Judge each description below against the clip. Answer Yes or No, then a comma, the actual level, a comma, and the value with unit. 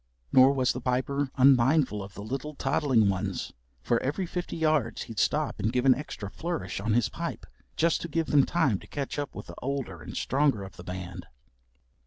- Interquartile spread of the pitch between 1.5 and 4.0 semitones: No, wide, 5.5 semitones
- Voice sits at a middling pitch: No, low, 130 Hz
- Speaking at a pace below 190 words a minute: No, average, 200 wpm